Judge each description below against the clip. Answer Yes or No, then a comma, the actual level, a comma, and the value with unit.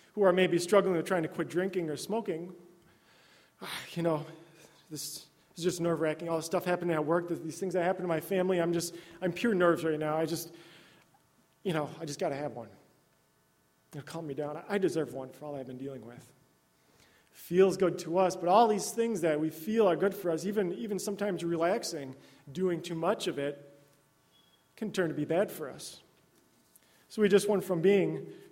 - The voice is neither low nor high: Yes, medium, 165 Hz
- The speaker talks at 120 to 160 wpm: No, fast, 205 wpm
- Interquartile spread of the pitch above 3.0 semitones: Yes, average, 3.9 semitones